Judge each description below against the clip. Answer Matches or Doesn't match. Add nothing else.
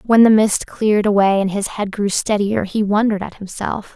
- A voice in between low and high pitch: Doesn't match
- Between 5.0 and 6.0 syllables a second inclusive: Matches